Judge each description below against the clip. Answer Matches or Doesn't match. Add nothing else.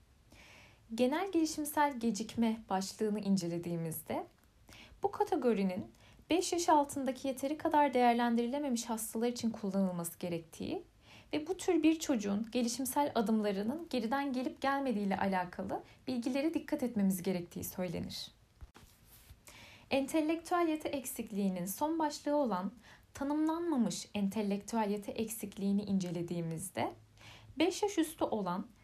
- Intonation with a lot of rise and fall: Matches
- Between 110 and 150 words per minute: Doesn't match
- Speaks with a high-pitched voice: Matches